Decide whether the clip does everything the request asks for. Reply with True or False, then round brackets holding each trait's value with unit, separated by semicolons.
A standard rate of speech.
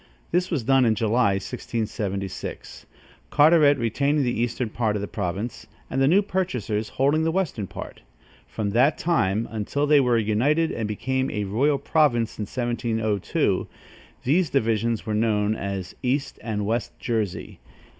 True (150 wpm)